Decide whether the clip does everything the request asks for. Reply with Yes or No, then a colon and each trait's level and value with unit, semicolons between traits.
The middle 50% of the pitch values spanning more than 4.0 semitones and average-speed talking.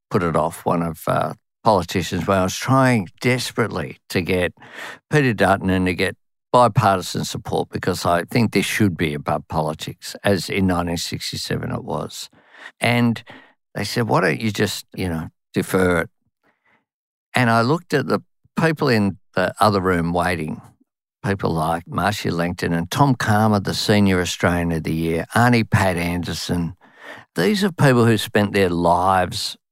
Yes: average, 5.3 semitones; average, 155 wpm